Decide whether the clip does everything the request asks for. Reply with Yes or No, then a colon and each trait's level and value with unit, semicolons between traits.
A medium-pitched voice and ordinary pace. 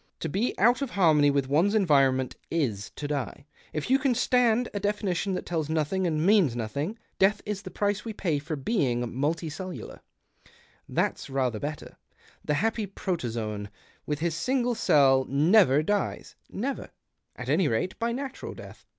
Yes: medium, 165 Hz; average, 165 wpm